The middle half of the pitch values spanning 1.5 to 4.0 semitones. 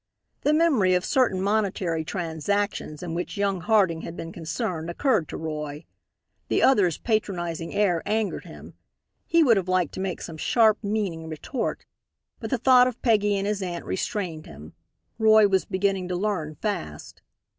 No: average, 4.4 semitones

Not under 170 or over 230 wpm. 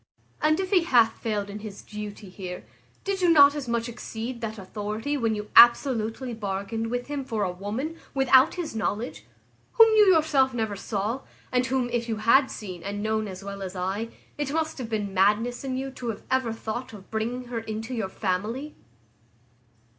Yes: average, 190 wpm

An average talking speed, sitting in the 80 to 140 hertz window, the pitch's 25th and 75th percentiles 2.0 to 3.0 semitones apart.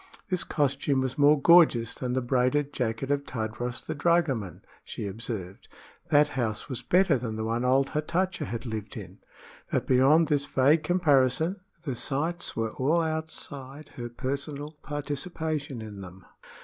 No: average, 150 wpm; low, 135 Hz; average, 4.2 semitones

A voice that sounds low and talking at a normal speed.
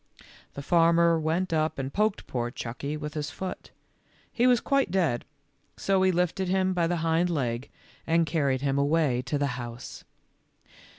No: medium, 160 Hz; average, 165 wpm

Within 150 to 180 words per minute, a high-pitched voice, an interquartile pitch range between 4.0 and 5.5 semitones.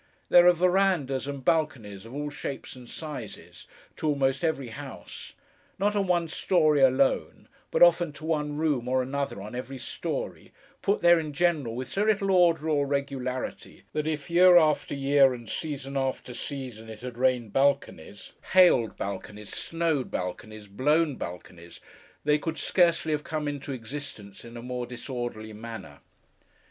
No: average, 155 wpm; medium, 140 Hz; average, 4.6 semitones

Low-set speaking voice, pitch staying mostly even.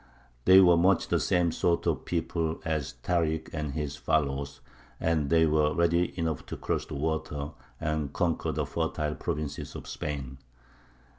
Yes: very low, 80 Hz; narrow, 2.1 semitones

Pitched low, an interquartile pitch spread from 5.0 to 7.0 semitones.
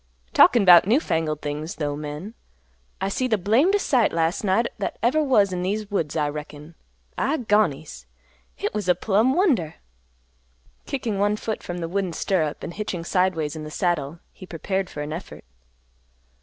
No: medium, 185 Hz; average, 5.3 semitones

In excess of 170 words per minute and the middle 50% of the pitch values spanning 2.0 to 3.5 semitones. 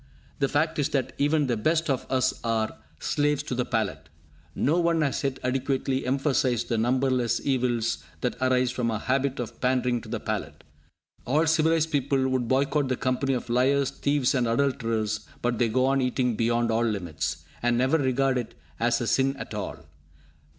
Yes: average, 180 wpm; narrow, 2.6 semitones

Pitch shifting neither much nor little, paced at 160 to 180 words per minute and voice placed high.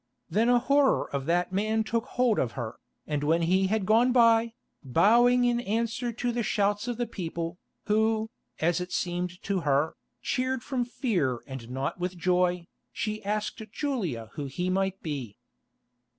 No: wide, 5.8 semitones; average, 165 wpm; high, 200 Hz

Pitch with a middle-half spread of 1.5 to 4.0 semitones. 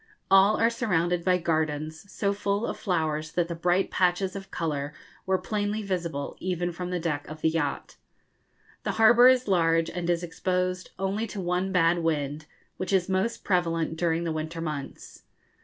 Yes: average, 2.9 semitones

